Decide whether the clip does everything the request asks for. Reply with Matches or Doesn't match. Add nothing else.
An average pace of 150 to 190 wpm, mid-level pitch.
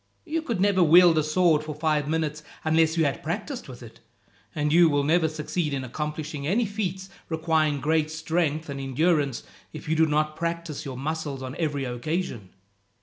Matches